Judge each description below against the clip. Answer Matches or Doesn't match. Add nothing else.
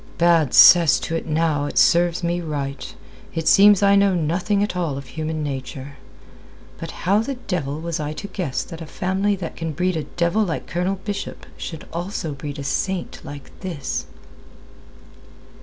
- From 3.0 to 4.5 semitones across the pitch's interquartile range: Matches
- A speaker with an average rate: Matches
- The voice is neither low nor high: Matches